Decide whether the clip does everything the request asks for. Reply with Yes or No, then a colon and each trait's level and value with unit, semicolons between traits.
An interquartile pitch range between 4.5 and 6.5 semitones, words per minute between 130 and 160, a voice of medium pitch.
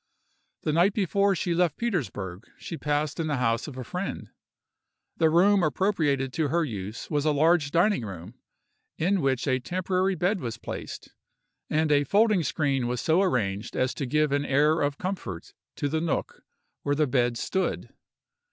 No: wide, 5.5 semitones; average, 170 wpm; medium, 150 Hz